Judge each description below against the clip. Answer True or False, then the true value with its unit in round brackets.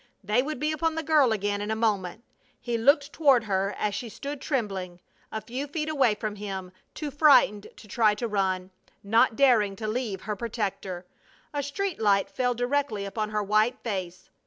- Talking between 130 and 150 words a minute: False (185 wpm)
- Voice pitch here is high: True (220 Hz)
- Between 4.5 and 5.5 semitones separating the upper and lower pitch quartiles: True (5.2 semitones)